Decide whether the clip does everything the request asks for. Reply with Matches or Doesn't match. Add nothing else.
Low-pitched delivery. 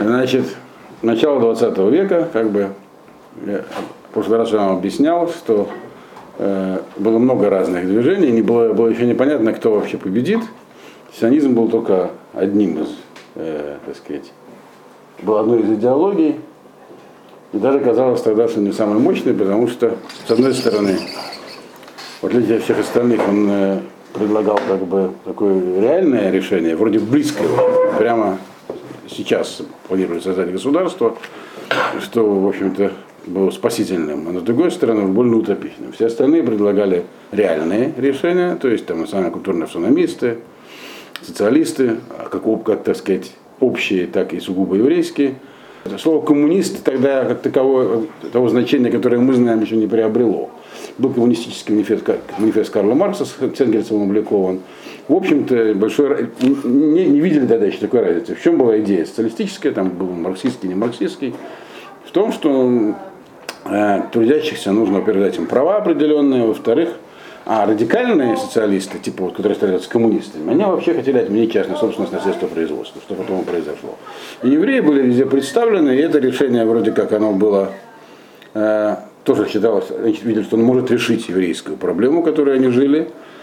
Matches